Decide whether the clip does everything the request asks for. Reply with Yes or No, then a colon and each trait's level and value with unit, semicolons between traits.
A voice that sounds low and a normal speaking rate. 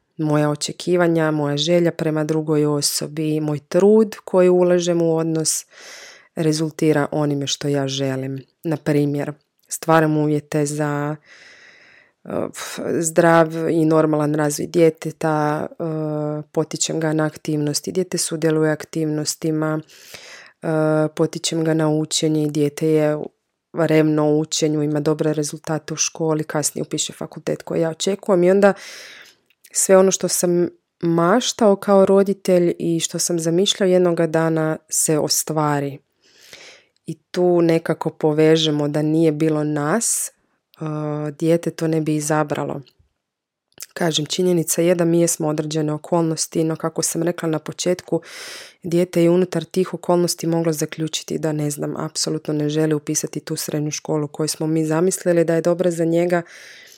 No: medium, 160 Hz; average, 135 wpm